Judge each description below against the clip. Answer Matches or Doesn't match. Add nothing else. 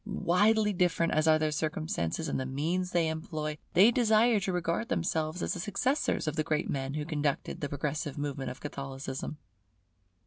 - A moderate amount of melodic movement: Matches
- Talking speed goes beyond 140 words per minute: Matches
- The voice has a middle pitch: Matches